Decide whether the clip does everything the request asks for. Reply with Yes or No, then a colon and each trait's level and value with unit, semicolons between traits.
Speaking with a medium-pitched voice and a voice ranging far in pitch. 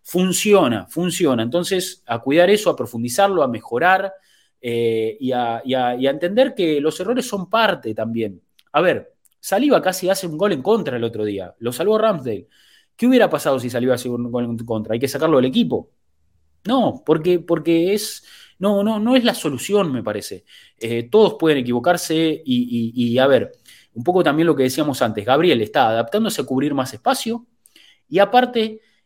Yes: medium, 160 Hz; wide, 9.0 semitones